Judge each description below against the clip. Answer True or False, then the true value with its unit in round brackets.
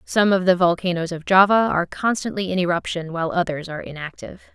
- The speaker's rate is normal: True (185 wpm)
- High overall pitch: False (180 Hz)